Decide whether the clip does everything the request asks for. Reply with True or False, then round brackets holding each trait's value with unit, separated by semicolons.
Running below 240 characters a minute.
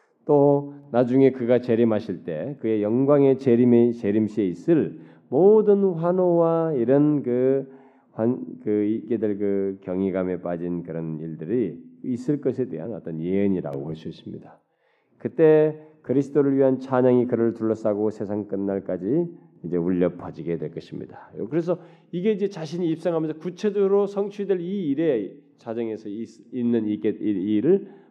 False (305 characters per minute)